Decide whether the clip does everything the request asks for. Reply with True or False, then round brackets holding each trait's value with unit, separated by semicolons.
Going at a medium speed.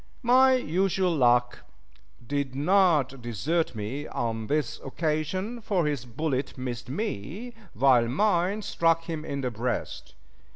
False (125 wpm)